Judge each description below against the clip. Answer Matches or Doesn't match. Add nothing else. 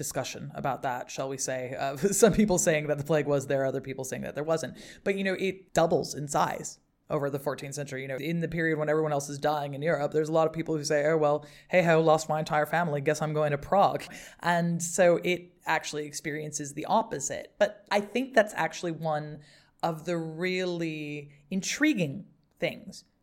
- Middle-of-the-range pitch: Matches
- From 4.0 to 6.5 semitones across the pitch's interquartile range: Doesn't match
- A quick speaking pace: Matches